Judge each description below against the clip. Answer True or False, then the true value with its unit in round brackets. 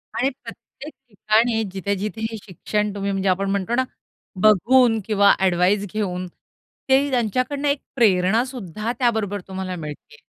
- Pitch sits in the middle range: False (210 Hz)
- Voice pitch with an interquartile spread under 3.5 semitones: False (3.9 semitones)